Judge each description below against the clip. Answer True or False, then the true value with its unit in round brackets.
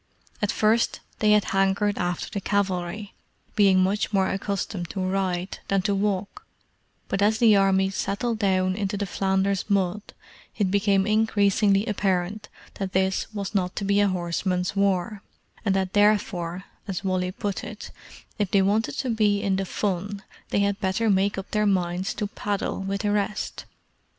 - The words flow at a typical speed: True (165 wpm)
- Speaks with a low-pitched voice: False (195 Hz)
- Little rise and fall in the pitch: True (1.5 semitones)